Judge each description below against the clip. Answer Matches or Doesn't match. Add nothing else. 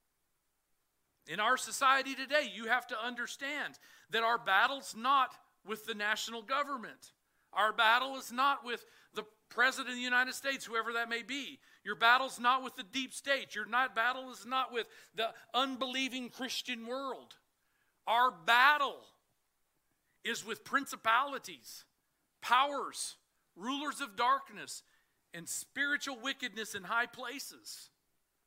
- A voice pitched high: Matches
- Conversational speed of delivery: Doesn't match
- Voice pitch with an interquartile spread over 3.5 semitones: Doesn't match